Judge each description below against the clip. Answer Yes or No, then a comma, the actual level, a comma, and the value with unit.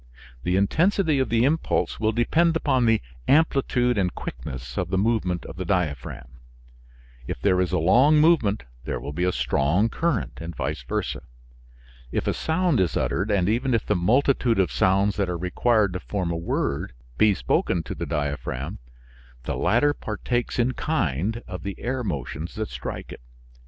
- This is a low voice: Yes, low, 100 Hz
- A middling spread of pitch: No, wide, 5.9 semitones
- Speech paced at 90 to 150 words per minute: No, average, 175 wpm